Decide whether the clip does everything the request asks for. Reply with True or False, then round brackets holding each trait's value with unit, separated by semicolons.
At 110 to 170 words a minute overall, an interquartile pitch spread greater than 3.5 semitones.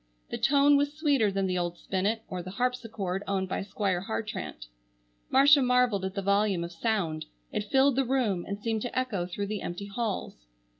False (190 wpm; 5.1 semitones)